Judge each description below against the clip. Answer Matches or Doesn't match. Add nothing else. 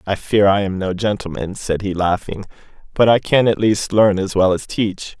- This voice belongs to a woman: Doesn't match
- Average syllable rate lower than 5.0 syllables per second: Matches